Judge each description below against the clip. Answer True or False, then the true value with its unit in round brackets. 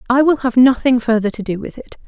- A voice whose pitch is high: True (240 Hz)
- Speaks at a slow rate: False (260 wpm)